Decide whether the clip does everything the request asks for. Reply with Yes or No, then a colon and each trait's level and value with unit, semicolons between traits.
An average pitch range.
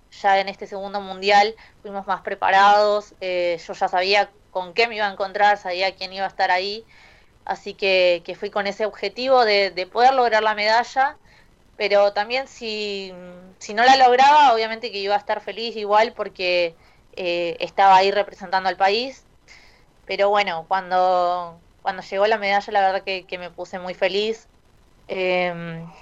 No: narrow, 2.2 semitones